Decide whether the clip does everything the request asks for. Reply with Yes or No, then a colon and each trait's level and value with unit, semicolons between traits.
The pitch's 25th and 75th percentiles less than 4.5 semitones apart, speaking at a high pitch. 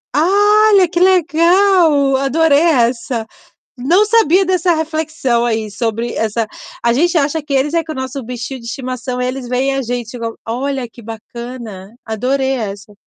No: wide, 5.5 semitones; very high, 265 Hz